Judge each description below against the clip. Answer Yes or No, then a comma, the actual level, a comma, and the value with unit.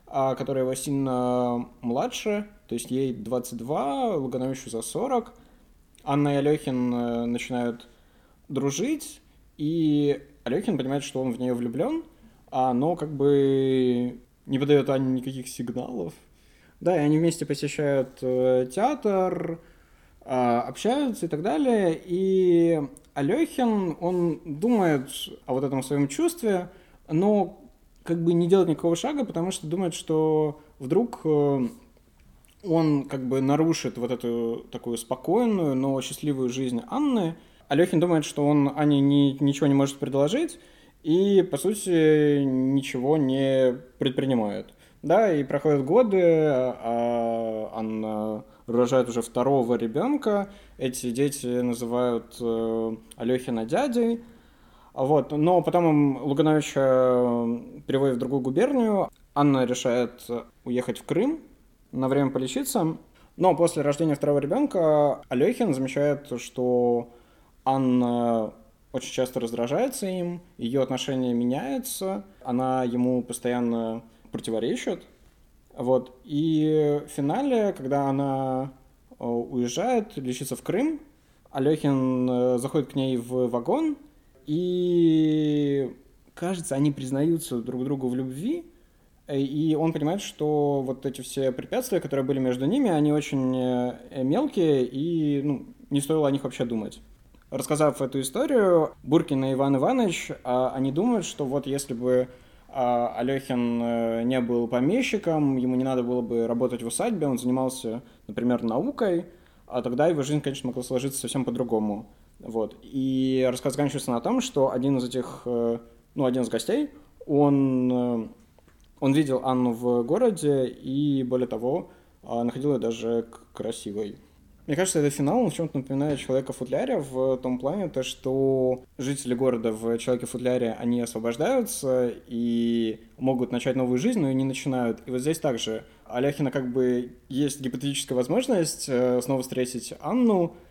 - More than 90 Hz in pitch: Yes, low, 135 Hz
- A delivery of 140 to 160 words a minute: No, average, 125 wpm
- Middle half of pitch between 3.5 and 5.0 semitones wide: Yes, average, 4.1 semitones